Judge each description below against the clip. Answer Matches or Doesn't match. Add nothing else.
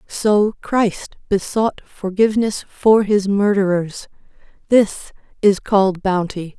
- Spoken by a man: Doesn't match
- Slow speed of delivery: Matches